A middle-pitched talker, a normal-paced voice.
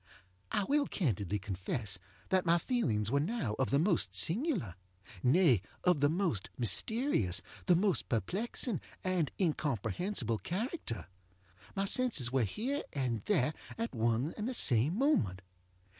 No: medium, 150 Hz; slow, 130 wpm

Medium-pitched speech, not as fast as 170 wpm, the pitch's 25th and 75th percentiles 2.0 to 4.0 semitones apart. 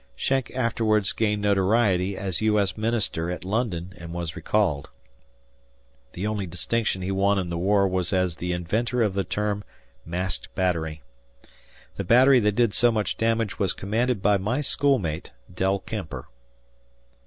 No: low, 100 Hz; average, 155 wpm; average, 3.6 semitones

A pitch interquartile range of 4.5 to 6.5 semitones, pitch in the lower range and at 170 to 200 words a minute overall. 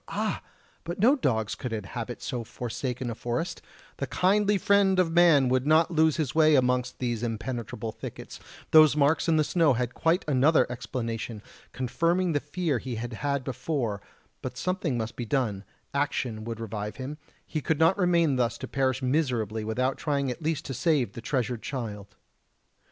Yes: average, 5.1 semitones; low, 130 Hz; average, 175 wpm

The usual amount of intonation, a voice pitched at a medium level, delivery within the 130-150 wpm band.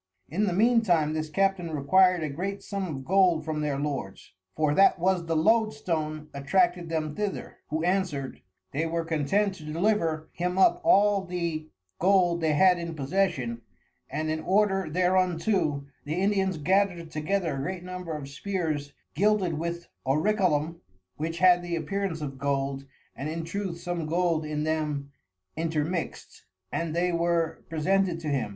No: average, 3.5 semitones; medium, 170 Hz; average, 160 wpm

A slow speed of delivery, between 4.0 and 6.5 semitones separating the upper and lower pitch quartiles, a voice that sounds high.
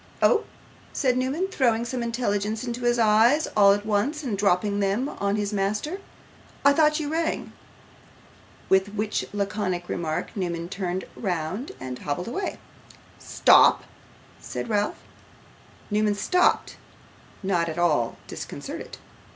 Yes: slow, 125 wpm; average, 4.6 semitones; high, 210 Hz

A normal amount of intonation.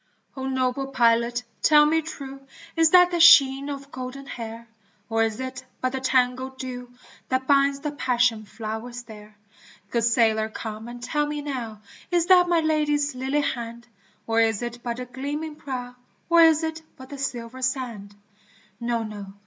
Yes: average, 3.5 semitones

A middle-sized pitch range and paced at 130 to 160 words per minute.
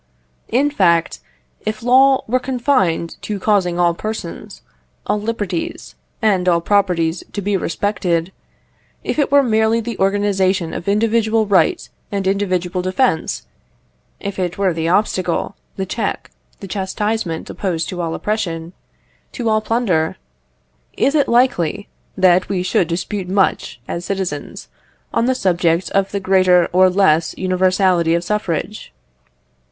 Yes: average, 3.5 semitones; slow, 135 wpm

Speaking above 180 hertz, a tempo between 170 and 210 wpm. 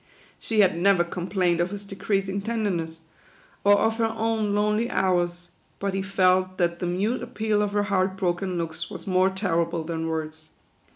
Yes: high, 190 Hz; average, 175 wpm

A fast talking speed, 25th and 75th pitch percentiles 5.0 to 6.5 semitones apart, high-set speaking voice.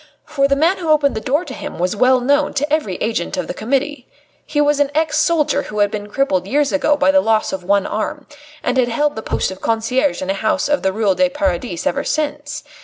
Yes: fast, 245 wpm; average, 5.3 semitones; very high, 275 Hz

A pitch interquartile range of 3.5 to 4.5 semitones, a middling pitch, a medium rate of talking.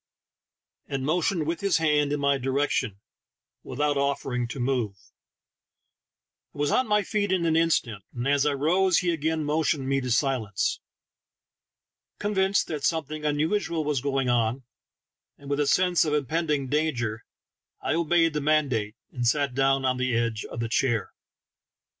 Yes: average, 3.9 semitones; medium, 145 Hz; average, 160 wpm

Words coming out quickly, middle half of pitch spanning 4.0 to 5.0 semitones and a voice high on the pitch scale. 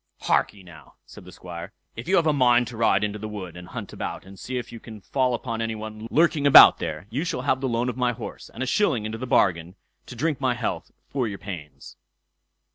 No: fast, 240 wpm; average, 4.3 semitones; low, 115 Hz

